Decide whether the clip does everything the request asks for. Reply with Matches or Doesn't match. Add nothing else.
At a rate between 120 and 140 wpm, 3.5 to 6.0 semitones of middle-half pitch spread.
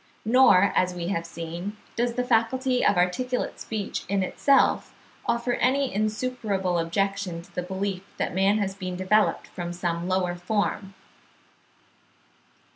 Matches